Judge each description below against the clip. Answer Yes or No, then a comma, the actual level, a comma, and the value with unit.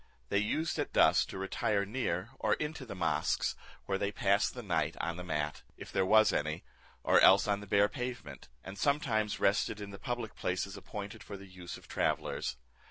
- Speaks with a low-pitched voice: Yes, low, 100 Hz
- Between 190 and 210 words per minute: Yes, average, 195 wpm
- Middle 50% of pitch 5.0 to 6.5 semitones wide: No, narrow, 2.4 semitones